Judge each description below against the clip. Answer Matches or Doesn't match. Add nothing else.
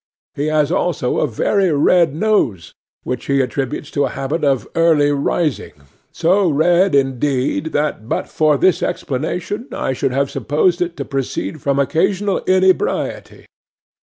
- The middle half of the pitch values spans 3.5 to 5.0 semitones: Matches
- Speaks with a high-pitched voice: Doesn't match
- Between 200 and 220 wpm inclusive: Doesn't match